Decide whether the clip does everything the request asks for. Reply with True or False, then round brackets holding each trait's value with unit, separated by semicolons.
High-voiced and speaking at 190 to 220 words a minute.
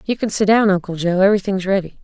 True (195 Hz; 205 wpm)